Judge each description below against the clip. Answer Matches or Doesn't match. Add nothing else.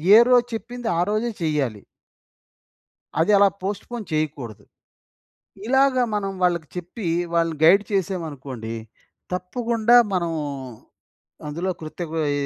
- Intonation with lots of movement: Matches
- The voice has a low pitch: Doesn't match